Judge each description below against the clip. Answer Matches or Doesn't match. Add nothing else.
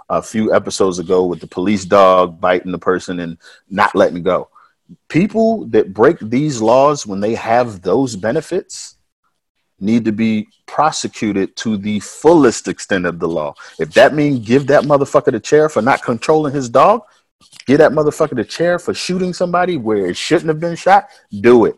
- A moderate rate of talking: Matches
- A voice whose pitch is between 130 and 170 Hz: Matches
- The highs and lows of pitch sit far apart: Matches